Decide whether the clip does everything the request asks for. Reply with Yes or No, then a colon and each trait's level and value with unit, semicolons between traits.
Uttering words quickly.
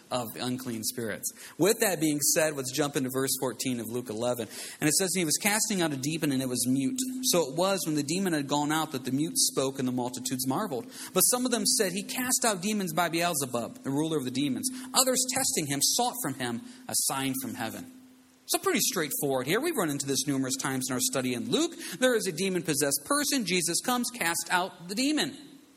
Yes: fast, 230 wpm